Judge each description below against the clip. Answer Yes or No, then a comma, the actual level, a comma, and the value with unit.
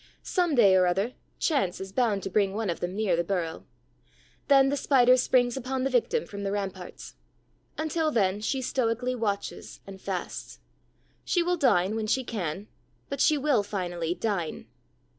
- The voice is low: No, high, 215 Hz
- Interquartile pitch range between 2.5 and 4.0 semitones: No, wide, 5.4 semitones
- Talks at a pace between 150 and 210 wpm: Yes, average, 170 wpm